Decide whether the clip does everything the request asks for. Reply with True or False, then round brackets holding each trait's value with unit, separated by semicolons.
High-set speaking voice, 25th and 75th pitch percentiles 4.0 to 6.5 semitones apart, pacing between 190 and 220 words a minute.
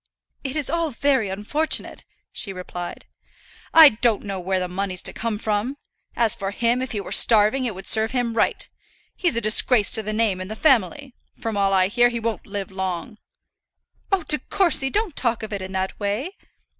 True (220 Hz; 4.8 semitones; 195 wpm)